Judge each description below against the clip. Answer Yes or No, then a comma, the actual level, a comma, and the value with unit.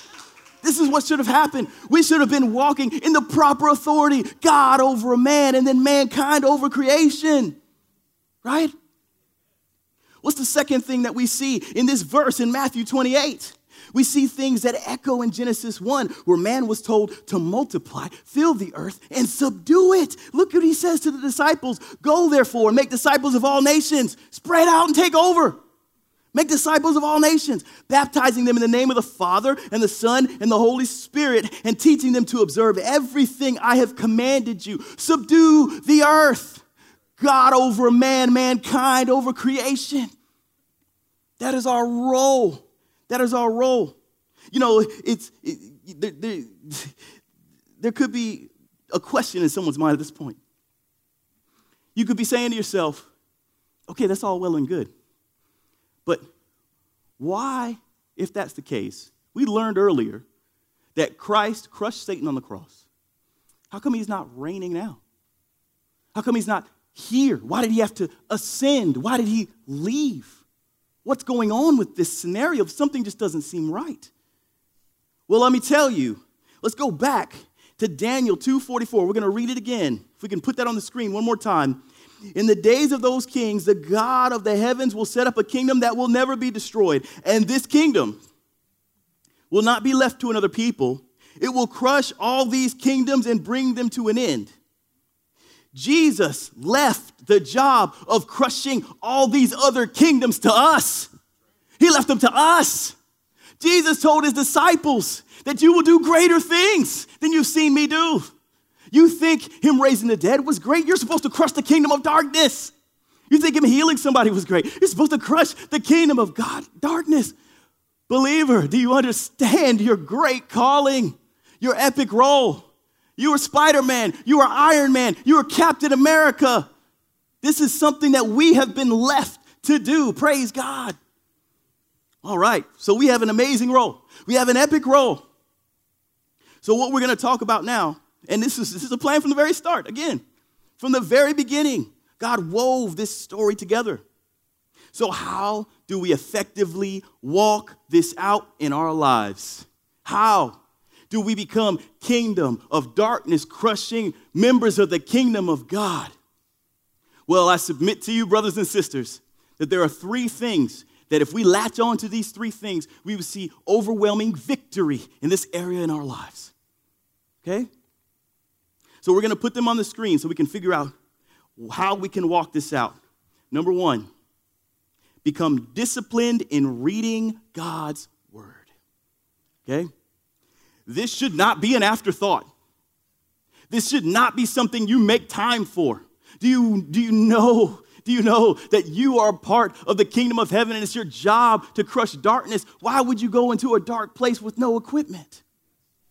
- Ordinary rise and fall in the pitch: Yes, average, 4.8 semitones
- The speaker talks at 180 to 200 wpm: No, average, 170 wpm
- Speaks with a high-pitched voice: Yes, very high, 250 Hz